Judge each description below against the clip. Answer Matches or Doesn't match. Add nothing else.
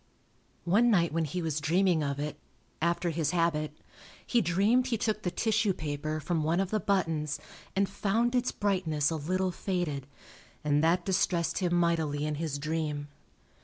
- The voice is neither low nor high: Matches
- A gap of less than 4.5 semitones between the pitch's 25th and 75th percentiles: Matches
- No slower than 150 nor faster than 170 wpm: Matches